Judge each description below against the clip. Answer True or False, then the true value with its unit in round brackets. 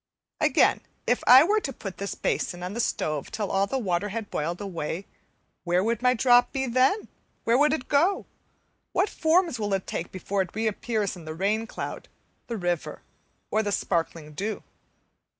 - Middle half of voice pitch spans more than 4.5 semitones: True (5.5 semitones)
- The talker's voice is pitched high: True (210 Hz)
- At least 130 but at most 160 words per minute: False (180 wpm)